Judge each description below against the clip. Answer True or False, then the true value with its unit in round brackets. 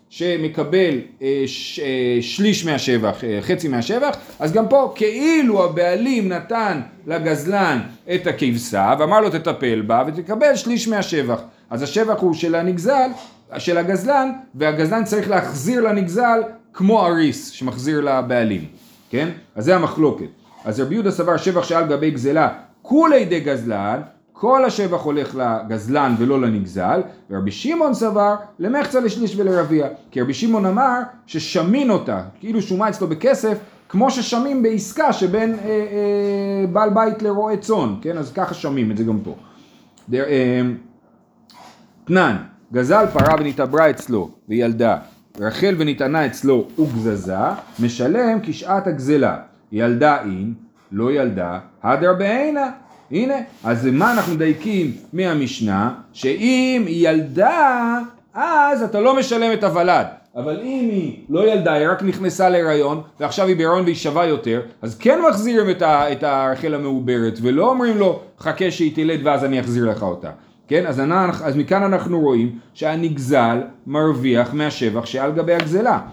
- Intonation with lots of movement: True (8.0 semitones)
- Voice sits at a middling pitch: True (170 Hz)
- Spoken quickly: False (135 wpm)